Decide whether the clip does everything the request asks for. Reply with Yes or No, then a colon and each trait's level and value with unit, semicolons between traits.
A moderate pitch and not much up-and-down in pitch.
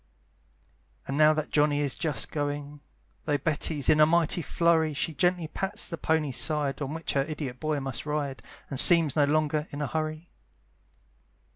Yes: medium, 150 Hz; narrow, 1.8 semitones